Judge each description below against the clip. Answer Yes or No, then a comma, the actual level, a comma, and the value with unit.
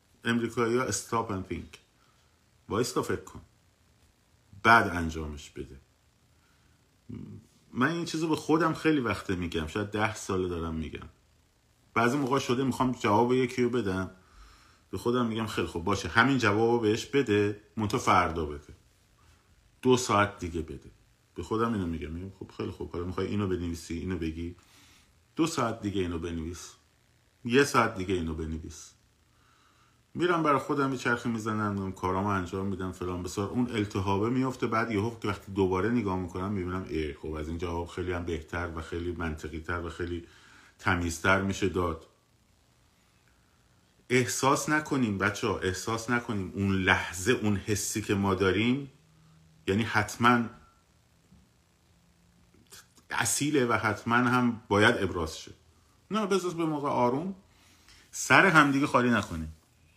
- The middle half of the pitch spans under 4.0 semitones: No, average, 5.1 semitones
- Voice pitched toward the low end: Yes, low, 100 Hz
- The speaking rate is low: No, average, 145 wpm